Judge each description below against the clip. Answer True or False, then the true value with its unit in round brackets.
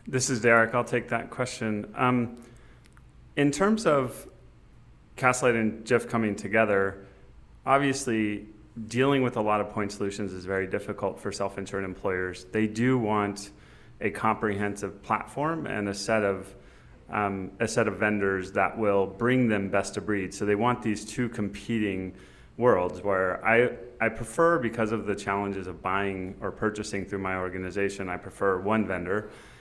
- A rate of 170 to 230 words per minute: False (160 wpm)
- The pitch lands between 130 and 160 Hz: False (105 Hz)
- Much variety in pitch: False (3.3 semitones)